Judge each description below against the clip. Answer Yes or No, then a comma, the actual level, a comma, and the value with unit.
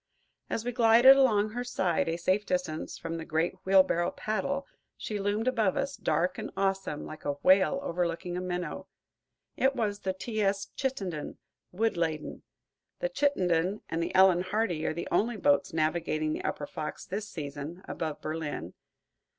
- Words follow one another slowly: No, average, 165 wpm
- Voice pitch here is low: No, medium, 185 Hz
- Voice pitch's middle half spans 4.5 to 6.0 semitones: Yes, average, 4.8 semitones